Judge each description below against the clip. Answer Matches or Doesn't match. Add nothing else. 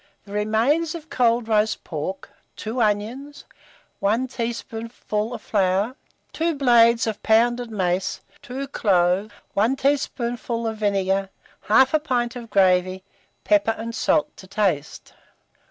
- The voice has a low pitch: Doesn't match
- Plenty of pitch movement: Doesn't match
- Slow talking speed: Matches